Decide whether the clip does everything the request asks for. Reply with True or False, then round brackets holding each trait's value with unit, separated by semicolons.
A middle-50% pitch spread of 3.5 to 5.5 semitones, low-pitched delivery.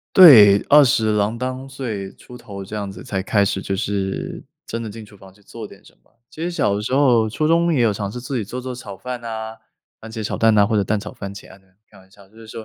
True (3.8 semitones; 110 Hz)